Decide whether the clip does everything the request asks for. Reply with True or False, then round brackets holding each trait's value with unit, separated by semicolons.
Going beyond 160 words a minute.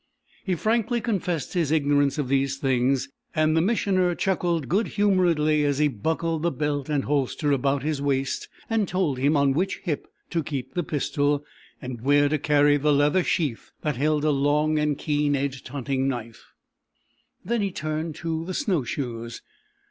True (170 wpm)